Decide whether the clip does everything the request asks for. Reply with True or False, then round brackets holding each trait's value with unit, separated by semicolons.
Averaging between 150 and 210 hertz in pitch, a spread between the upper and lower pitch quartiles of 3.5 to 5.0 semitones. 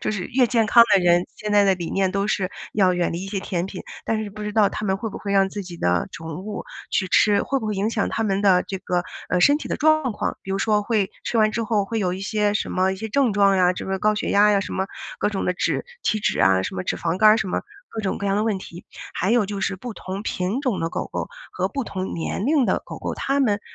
False (200 Hz; 2.4 semitones)